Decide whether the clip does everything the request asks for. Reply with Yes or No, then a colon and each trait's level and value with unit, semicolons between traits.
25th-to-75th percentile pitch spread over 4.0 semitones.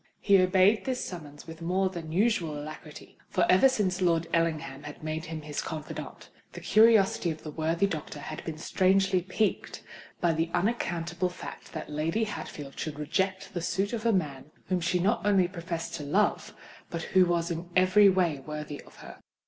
No: average, 3.4 semitones